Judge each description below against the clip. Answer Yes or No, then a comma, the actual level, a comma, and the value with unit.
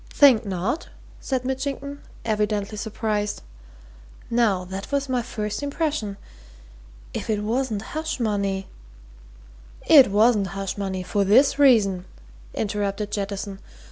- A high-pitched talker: Yes, high, 210 Hz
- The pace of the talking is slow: Yes, slow, 115 wpm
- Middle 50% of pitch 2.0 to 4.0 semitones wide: No, average, 4.5 semitones